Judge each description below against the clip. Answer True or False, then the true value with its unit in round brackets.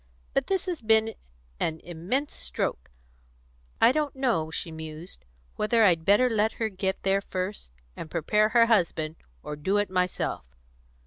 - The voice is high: True (200 Hz)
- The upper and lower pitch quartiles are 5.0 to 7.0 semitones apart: True (5.5 semitones)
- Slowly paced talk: False (150 wpm)